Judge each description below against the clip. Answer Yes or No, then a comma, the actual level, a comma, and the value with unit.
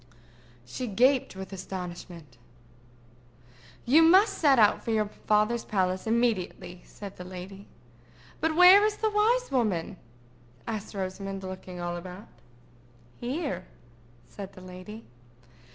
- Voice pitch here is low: No, high, 205 Hz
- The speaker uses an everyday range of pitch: No, wide, 5.8 semitones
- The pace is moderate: No, slow, 120 wpm